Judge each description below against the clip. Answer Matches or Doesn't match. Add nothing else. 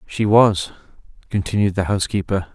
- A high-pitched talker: Doesn't match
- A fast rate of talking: Doesn't match